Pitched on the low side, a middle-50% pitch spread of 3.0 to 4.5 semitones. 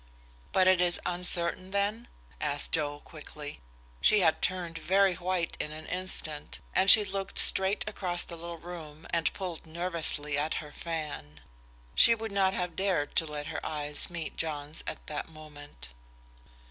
No: medium, 170 Hz; average, 3.6 semitones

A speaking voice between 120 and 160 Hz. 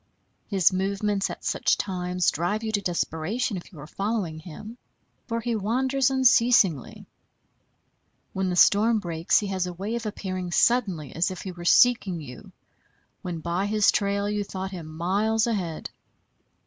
No: high, 195 Hz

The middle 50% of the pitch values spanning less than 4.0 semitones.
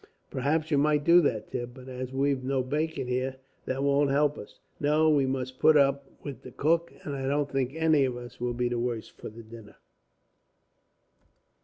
Yes: narrow, 2.6 semitones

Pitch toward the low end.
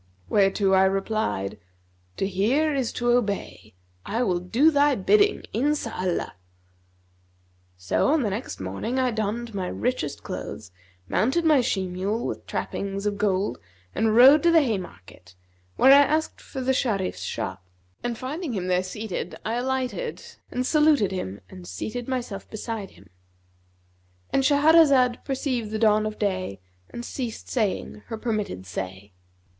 No: high, 215 Hz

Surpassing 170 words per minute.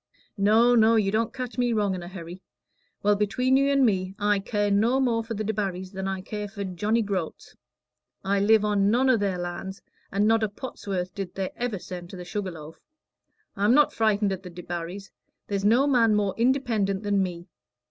Yes: fast, 205 wpm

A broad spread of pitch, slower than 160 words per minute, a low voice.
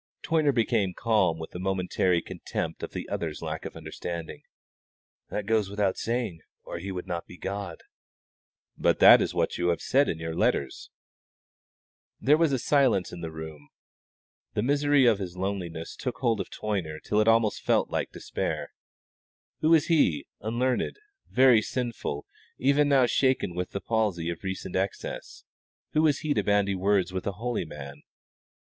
No: wide, 5.9 semitones; average, 165 wpm; low, 100 Hz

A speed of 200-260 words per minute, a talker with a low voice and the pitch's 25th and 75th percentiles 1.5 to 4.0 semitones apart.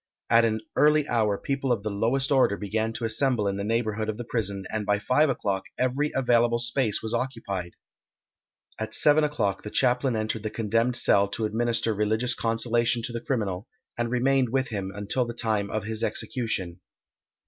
No: average, 180 wpm; low, 115 Hz; average, 2.9 semitones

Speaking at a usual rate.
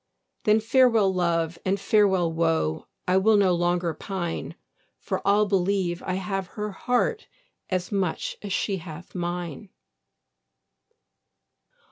No: slow, 120 wpm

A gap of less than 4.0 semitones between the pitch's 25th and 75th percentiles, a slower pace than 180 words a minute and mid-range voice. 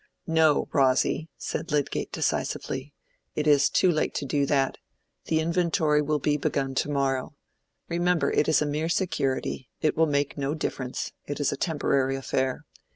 Yes: average, 2.7 semitones; average, 160 wpm; medium, 145 Hz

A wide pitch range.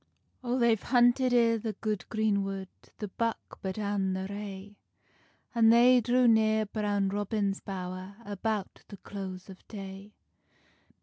No: narrow, 2.6 semitones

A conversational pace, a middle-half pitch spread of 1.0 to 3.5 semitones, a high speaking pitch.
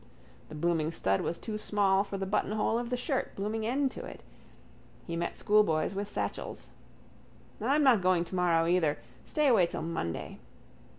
No: average, 165 wpm; average, 4.7 semitones; high, 195 Hz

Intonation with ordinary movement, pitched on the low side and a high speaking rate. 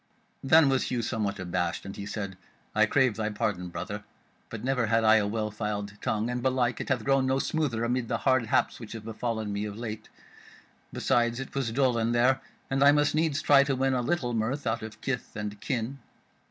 Yes: average, 3.7 semitones; low, 120 Hz; fast, 215 wpm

